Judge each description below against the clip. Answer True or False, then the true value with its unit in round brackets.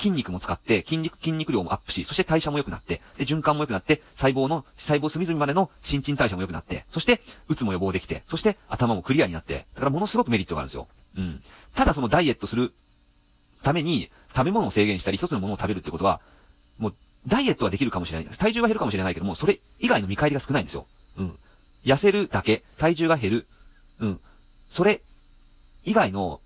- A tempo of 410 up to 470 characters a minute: True (460 characters per minute)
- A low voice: True (120 Hz)